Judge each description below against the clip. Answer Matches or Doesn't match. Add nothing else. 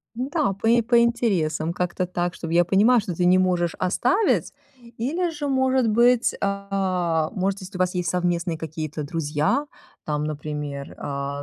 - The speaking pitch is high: Doesn't match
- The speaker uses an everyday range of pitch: Doesn't match